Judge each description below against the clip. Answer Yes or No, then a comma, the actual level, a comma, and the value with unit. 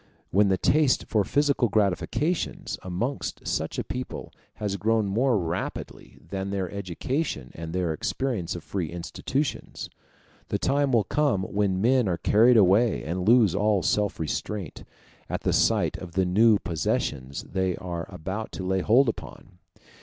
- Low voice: Yes, low, 100 Hz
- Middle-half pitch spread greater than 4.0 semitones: Yes, average, 4.5 semitones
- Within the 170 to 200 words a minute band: No, average, 155 wpm